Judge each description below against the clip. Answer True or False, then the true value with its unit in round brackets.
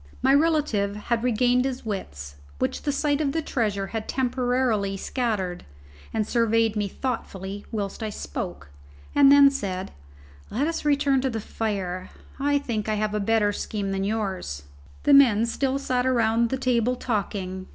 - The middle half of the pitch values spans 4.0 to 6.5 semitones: True (4.6 semitones)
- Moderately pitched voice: False (225 Hz)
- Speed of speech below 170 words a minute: True (160 wpm)